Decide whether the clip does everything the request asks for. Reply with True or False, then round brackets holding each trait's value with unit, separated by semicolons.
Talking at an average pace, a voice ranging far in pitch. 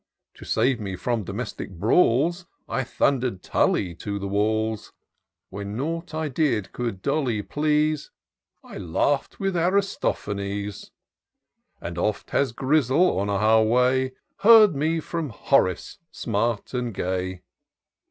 False (125 wpm; 6.8 semitones)